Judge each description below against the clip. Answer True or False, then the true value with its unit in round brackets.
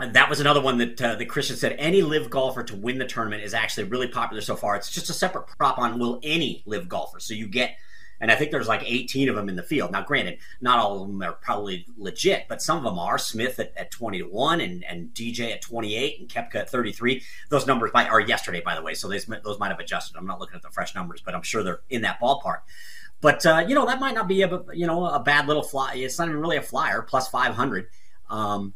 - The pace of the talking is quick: True (260 wpm)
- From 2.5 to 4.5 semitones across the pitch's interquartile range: False (5.6 semitones)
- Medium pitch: False (130 Hz)